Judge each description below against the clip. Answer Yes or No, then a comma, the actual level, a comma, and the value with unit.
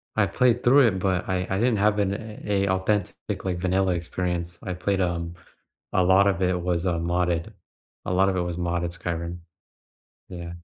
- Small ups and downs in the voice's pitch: Yes, narrow, 2.1 semitones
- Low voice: Yes, very low, 90 Hz